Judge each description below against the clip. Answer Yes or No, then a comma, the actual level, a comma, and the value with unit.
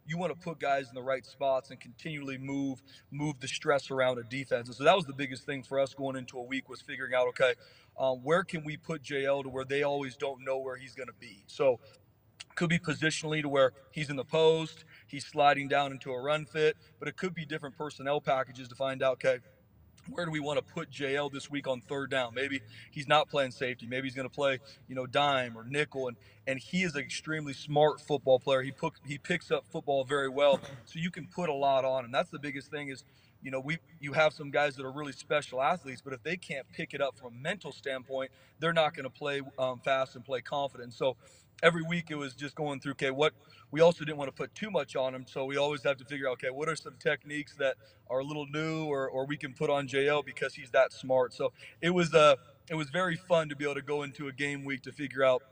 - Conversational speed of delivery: No, fast, 260 wpm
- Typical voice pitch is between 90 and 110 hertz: No, medium, 140 Hz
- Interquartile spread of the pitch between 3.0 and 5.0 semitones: No, narrow, 2.4 semitones